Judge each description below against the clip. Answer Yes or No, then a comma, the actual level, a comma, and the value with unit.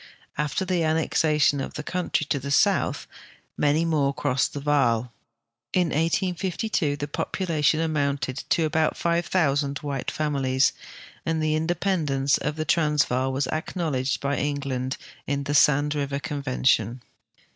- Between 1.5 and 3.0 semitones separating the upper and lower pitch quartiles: Yes, narrow, 2.4 semitones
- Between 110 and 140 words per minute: Yes, slow, 135 wpm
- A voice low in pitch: No, medium, 145 Hz